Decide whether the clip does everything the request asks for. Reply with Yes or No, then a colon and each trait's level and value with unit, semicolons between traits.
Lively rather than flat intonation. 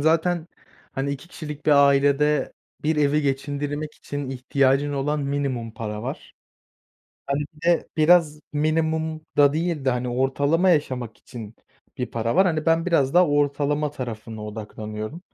No: average, 3.0 semitones